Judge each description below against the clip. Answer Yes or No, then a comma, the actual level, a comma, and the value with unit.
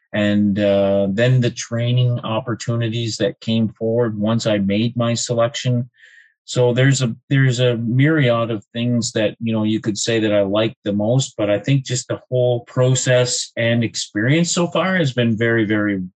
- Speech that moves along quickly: No, average, 180 wpm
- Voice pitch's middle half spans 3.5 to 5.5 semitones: No, narrow, 2.4 semitones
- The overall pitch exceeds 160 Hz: No, low, 115 Hz